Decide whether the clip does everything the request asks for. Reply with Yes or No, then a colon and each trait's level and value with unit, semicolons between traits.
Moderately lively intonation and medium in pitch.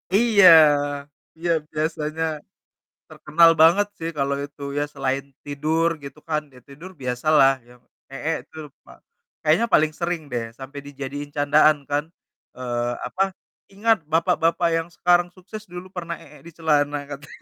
Yes: average, 3.1 semitones; medium, 155 Hz